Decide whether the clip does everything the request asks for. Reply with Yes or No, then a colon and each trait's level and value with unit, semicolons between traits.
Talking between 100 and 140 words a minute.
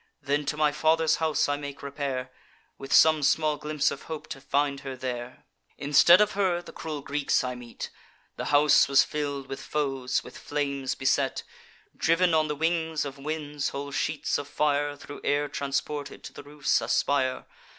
No: average, 175 wpm